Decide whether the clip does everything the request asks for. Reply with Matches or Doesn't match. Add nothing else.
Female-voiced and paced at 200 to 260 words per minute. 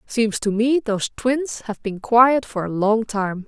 Matches